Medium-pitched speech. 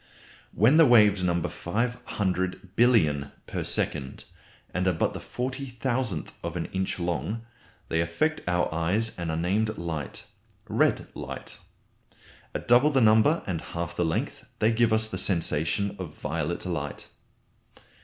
No: very low, 95 Hz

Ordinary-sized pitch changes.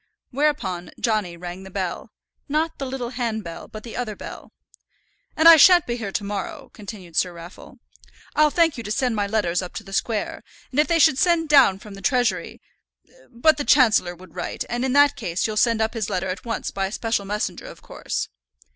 No: wide, 5.7 semitones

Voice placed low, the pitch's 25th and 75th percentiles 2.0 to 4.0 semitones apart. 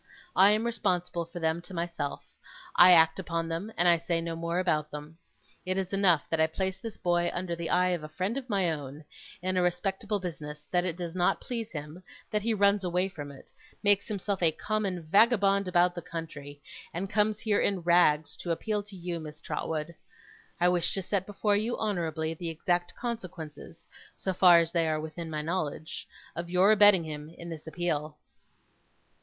No: medium, 175 Hz; average, 3.1 semitones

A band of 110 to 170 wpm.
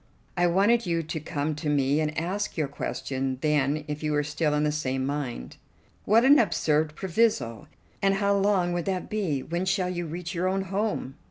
No: average, 195 wpm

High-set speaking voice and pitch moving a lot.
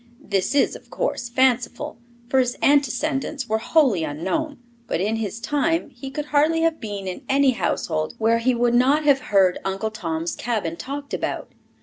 Yes: high, 245 Hz; wide, 5.8 semitones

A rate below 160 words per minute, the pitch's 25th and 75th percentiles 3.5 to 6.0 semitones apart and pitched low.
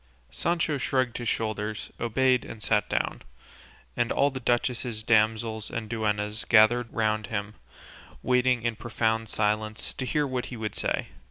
No: average, 150 wpm; narrow, 2.4 semitones; low, 115 Hz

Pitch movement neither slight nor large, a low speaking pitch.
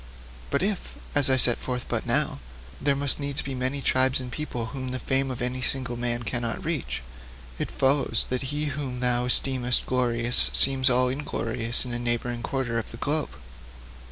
No: narrow, 2.1 semitones; low, 130 Hz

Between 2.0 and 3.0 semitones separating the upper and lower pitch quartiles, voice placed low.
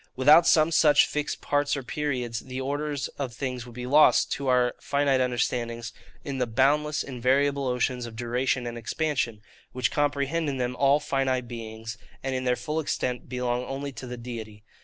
Yes: average, 2.7 semitones; low, 130 Hz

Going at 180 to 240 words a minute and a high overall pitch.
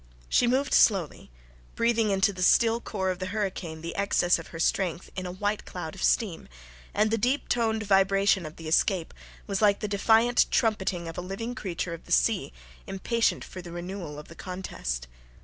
Yes: average, 190 wpm; high, 195 Hz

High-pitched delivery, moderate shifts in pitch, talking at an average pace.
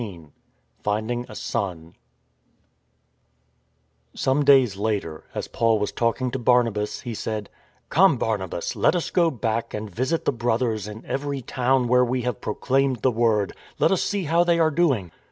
No: low, 120 Hz; average, 4.0 semitones; average, 165 wpm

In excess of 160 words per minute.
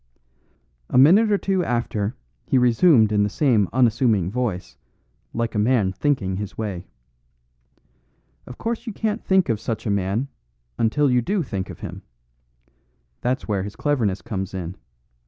No: average, 155 wpm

